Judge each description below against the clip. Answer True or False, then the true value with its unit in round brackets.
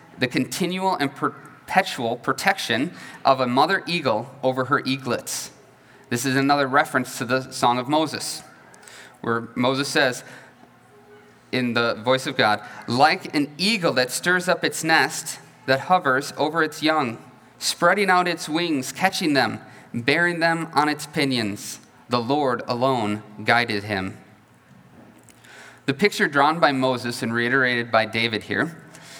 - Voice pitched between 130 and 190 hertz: True (135 Hz)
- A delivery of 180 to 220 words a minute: False (140 wpm)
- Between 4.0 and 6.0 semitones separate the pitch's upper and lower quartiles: True (4.4 semitones)